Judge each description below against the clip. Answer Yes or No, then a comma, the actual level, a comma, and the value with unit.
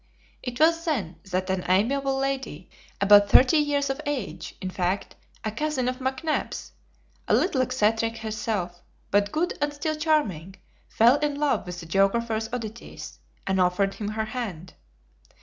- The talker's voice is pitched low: No, high, 225 Hz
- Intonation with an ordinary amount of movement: No, wide, 6.2 semitones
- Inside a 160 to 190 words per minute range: No, average, 150 wpm